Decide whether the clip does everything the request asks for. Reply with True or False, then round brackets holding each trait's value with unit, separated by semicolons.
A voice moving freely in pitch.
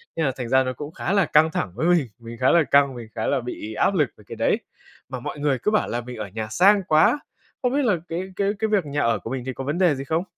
True (6.2 semitones)